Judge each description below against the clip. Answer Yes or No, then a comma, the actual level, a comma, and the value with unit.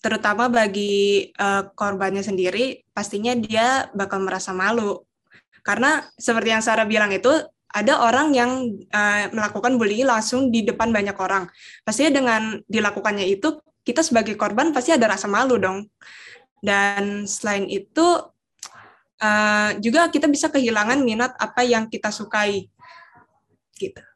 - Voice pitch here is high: Yes, high, 220 Hz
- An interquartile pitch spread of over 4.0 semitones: No, average, 3.5 semitones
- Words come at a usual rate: Yes, average, 130 wpm